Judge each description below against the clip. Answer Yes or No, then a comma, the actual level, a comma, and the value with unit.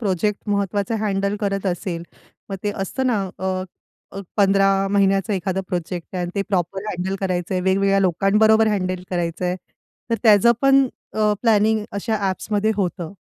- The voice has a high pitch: Yes, high, 195 Hz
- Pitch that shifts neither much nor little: No, narrow, 2.2 semitones